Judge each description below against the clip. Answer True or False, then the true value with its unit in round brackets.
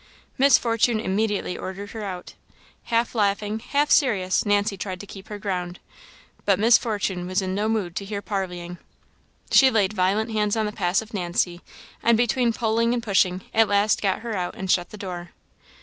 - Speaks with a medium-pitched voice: False (205 Hz)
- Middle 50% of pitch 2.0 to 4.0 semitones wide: True (3.1 semitones)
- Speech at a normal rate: True (180 wpm)